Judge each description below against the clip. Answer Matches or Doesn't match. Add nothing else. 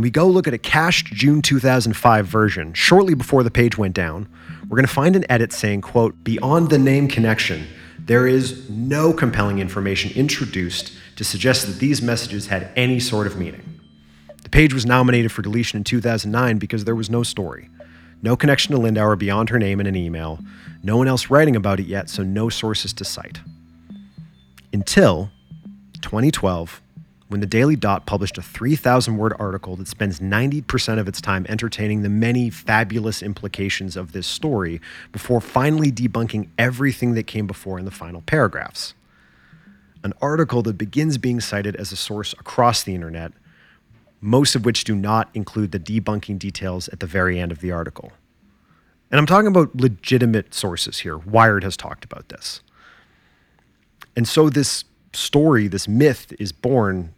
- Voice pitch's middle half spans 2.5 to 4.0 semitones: Doesn't match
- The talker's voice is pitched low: Matches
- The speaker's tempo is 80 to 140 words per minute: Doesn't match